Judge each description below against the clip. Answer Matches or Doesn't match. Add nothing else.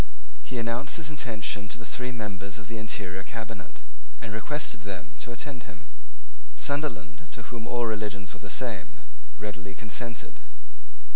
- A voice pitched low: Matches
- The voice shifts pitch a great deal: Doesn't match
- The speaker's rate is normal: Matches